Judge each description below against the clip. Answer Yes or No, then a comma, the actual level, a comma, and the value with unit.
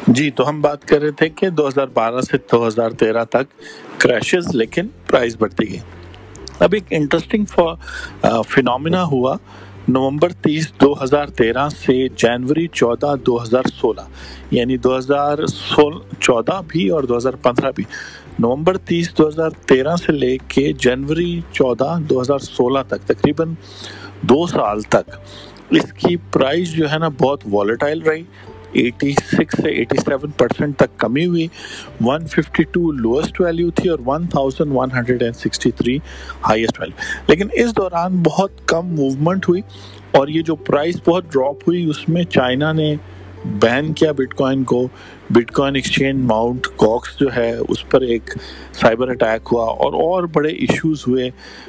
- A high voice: No, medium, 140 Hz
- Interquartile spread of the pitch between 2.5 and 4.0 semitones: No, average, 5.1 semitones